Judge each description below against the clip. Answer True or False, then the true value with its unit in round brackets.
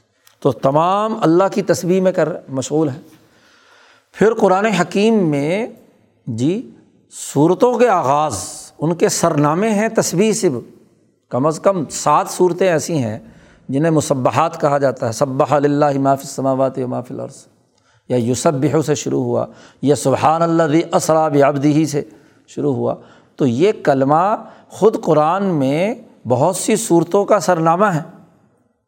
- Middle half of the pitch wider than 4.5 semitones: True (5.3 semitones)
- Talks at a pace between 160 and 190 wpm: False (150 wpm)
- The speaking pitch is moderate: True (160 Hz)